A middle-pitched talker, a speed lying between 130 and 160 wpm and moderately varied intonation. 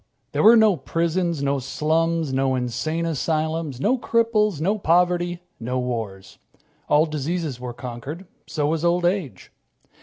Yes: medium, 160 Hz; average, 140 wpm; average, 4.6 semitones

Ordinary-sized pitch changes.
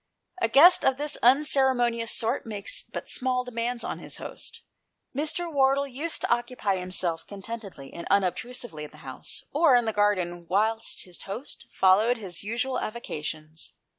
No: wide, 5.7 semitones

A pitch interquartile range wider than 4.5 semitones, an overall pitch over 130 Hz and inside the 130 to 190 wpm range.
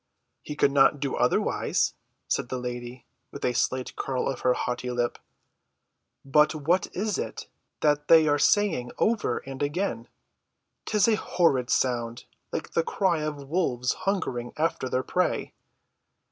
Yes: average, 5.0 semitones; medium, 140 Hz; average, 145 wpm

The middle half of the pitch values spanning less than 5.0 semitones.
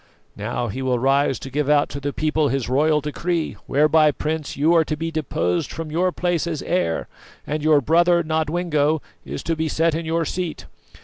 Yes: narrow, 2.5 semitones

